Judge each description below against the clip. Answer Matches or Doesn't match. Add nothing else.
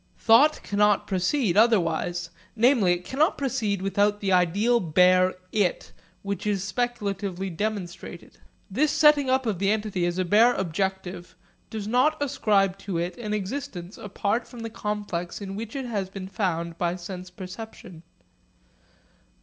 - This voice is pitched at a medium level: Doesn't match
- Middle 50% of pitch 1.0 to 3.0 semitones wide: Doesn't match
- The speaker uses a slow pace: Doesn't match